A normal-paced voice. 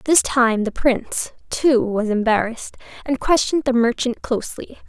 Yes: average, 150 wpm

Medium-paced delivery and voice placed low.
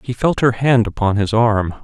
No: fast, 230 wpm; low, 110 Hz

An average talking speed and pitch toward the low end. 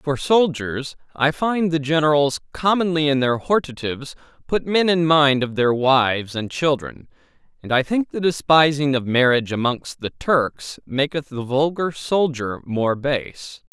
No: average, 155 wpm; medium, 145 Hz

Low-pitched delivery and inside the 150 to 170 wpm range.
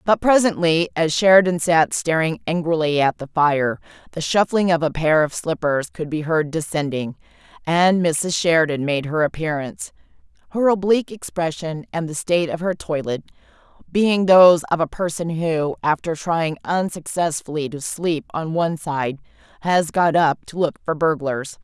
No: medium, 165 Hz; average, 160 wpm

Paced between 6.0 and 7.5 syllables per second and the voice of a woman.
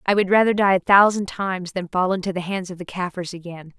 Yes: 6.1 syllables/s; female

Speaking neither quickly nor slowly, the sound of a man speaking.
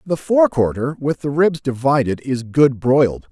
Yes: average, 180 wpm; male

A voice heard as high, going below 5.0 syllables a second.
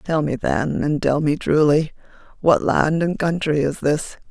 No: medium, 150 Hz; 4.1 syllables/s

